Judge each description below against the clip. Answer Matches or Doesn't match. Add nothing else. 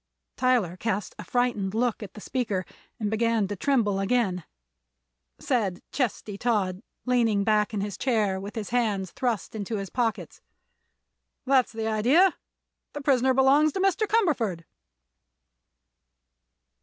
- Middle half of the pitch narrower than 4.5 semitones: Matches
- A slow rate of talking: Matches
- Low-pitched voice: Doesn't match